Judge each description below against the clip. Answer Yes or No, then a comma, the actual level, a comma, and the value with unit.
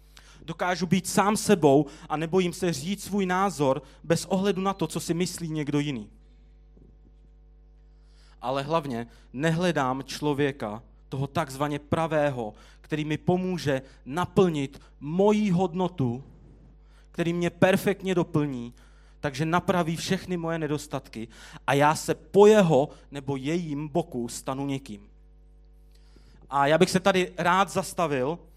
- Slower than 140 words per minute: Yes, average, 120 wpm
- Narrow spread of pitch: No, average, 5.0 semitones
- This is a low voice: No, medium, 150 Hz